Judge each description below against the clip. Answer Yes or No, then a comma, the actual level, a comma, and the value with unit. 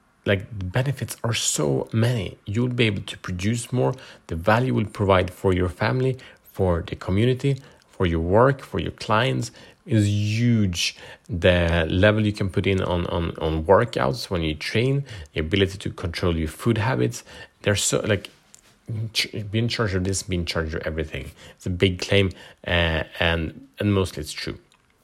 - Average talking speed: Yes, average, 175 wpm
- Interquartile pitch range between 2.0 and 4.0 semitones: No, average, 4.5 semitones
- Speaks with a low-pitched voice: Yes, very low, 95 Hz